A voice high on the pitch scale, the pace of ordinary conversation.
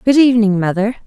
Yes: high, 220 Hz; average, 170 wpm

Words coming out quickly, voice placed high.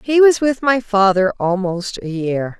No: average, 185 wpm; high, 210 Hz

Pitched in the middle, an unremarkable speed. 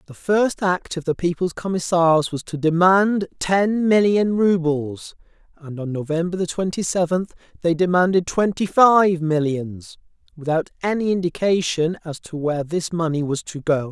Yes: medium, 170 Hz; average, 145 wpm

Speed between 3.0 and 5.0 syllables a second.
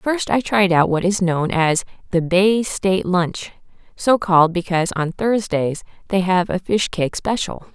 Yes: 4.5 syllables/s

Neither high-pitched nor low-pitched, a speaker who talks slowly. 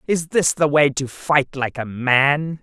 No: medium, 145 Hz; fast, 205 wpm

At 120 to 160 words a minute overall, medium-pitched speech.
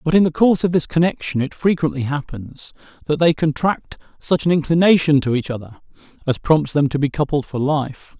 No: average, 200 wpm; medium, 150 Hz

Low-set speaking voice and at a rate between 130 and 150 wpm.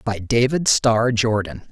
Yes: low, 115 Hz; average, 140 wpm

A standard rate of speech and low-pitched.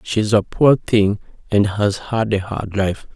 Yes: average, 190 wpm; low, 105 Hz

